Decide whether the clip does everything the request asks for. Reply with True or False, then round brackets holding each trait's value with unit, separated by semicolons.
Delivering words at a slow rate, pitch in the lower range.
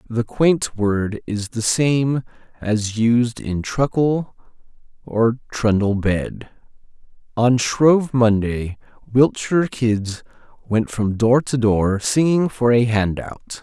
True (120 wpm; 115 Hz)